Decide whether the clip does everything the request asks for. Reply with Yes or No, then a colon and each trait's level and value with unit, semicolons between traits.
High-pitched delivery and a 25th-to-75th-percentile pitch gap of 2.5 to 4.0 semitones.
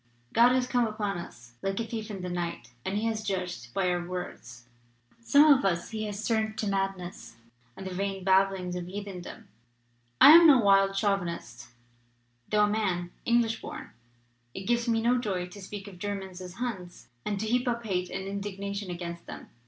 Yes: high, 195 Hz; average, 3.4 semitones